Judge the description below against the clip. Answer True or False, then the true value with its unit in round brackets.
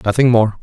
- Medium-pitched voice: False (115 Hz)